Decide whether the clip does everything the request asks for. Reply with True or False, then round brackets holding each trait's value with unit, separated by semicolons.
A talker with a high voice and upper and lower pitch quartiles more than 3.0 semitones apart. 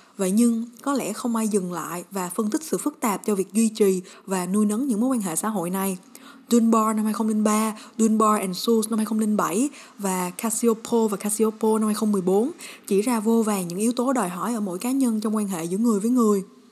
False (220 Hz; 2.7 semitones)